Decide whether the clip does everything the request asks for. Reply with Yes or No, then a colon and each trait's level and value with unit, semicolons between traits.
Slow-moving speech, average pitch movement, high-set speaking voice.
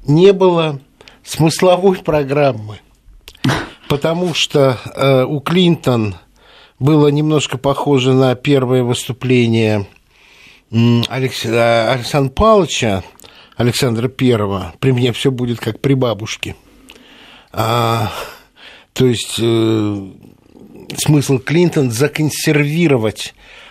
No: slow, 85 wpm; average, 4.4 semitones; low, 130 Hz